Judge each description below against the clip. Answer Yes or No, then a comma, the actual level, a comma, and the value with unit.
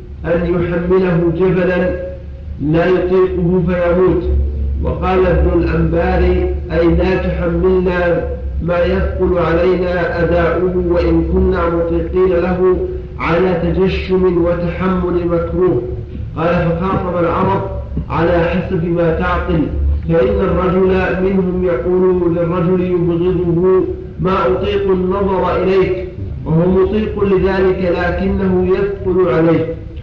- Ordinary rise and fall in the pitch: No, narrow, 1.5 semitones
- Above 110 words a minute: No, average, 95 wpm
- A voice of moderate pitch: Yes, medium, 175 Hz